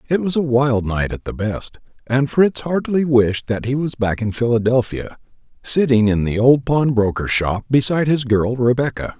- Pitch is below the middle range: Yes, low, 125 Hz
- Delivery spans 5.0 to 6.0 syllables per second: No, 4.8 syllables/s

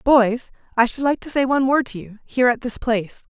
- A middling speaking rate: No, fast, 250 wpm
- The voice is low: No, high, 245 Hz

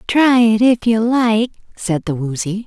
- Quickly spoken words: No, average, 180 wpm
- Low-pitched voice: No, high, 220 Hz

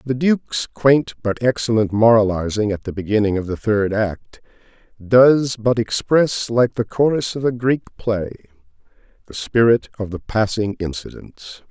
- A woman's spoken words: No, male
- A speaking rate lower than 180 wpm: Yes, average, 150 wpm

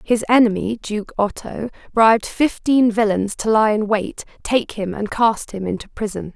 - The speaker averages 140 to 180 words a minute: Yes, average, 170 wpm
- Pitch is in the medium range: No, high, 215 Hz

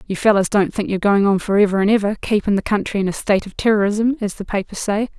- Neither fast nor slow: No, fast, 265 wpm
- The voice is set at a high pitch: Yes, high, 205 Hz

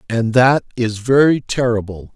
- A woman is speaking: No, male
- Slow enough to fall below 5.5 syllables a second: Yes, 4.3 syllables/s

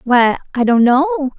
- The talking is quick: No, average, 175 wpm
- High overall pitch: Yes, very high, 270 Hz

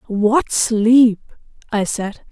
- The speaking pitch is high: Yes, high, 225 Hz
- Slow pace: Yes, slow, 105 wpm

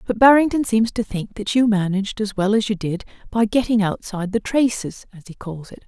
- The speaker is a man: No, female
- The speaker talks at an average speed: No, fast, 225 wpm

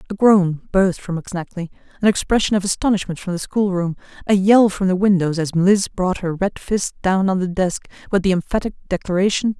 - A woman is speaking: Yes, female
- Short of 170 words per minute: No, average, 195 wpm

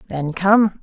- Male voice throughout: No, female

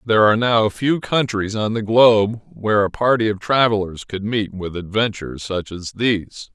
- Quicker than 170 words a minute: Yes, average, 185 wpm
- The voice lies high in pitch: No, low, 105 Hz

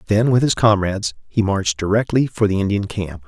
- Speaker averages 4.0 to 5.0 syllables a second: No, 5.8 syllables/s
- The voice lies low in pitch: Yes, low, 100 Hz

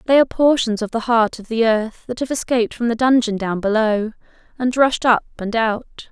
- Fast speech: Yes, fast, 215 wpm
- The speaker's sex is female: Yes, female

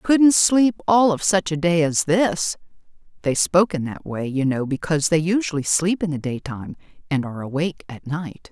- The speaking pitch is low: No, medium, 165 Hz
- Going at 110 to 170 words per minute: No, average, 195 wpm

